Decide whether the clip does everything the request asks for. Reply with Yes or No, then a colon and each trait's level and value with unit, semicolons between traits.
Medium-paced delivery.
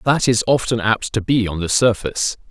No: fast, 215 wpm